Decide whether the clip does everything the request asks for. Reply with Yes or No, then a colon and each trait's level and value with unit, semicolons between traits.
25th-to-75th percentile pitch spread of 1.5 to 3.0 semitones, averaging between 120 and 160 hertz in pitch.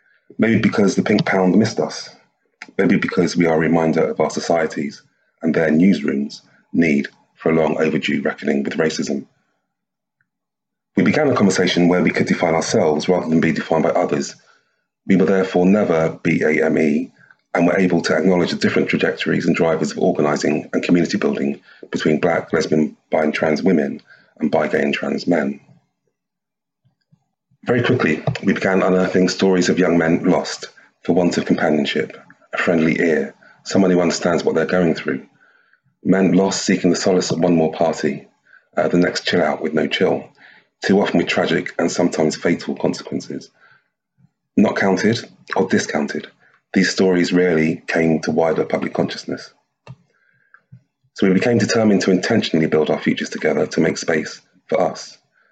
No: average, 2.7 semitones; very low, 85 Hz